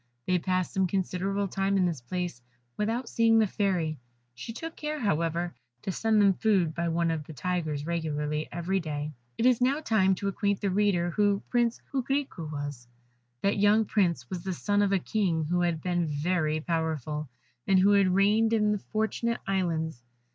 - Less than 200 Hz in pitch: Yes, medium, 185 Hz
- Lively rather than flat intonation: No, average, 4.2 semitones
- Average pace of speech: Yes, average, 185 wpm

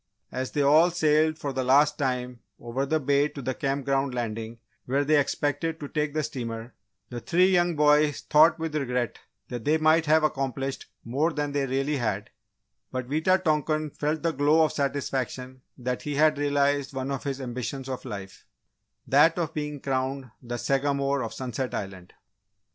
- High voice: No, medium, 140 Hz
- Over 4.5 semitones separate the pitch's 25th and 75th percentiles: No, average, 2.9 semitones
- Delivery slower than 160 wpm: No, average, 175 wpm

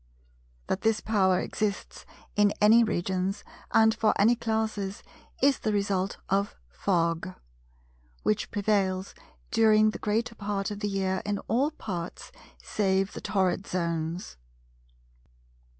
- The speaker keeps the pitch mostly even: Yes, narrow, 2.3 semitones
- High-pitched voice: Yes, high, 200 Hz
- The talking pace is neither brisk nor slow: No, slow, 120 wpm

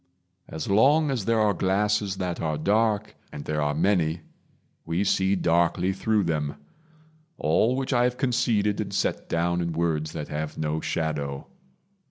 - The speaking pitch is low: Yes, very low, 90 Hz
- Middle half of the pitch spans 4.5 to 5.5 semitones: Yes, average, 5.2 semitones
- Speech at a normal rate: Yes, average, 160 wpm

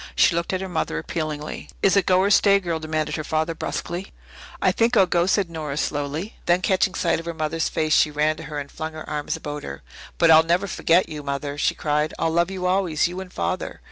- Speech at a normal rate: No, fast, 235 wpm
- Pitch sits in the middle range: Yes, medium, 165 Hz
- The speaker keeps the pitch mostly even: No, average, 3.1 semitones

